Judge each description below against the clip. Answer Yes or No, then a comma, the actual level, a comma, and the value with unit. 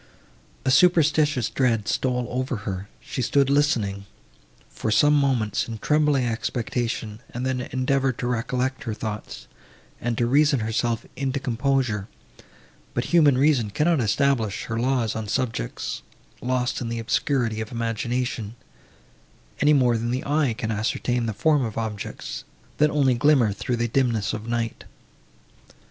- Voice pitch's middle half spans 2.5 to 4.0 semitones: Yes, average, 3.4 semitones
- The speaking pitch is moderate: No, low, 125 Hz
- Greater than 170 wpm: No, average, 145 wpm